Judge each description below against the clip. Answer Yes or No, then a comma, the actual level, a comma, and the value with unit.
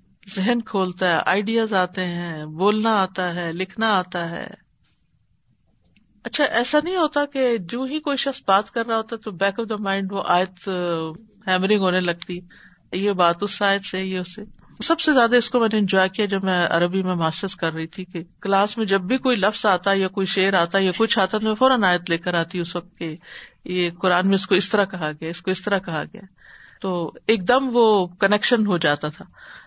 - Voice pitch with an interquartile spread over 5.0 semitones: No, average, 3.4 semitones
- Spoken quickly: Yes, fast, 215 wpm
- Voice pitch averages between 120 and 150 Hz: No, high, 195 Hz